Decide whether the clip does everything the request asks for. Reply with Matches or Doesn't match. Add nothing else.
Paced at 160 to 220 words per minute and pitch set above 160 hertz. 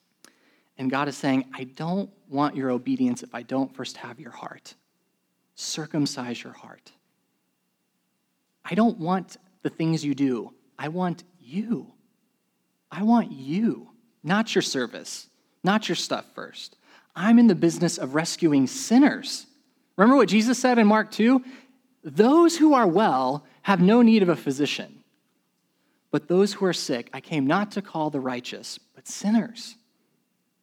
Doesn't match